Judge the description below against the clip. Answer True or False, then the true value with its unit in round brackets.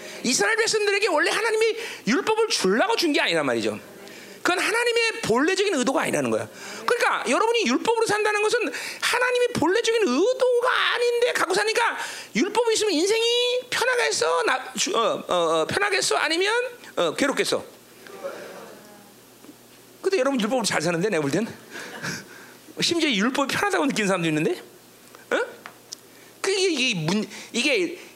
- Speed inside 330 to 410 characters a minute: True (340 characters per minute)